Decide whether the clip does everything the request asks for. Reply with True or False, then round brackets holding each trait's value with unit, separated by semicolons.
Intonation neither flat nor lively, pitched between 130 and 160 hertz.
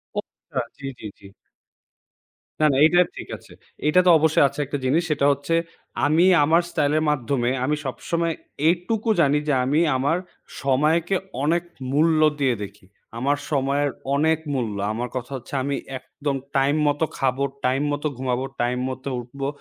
True (3.1 semitones; 140 Hz)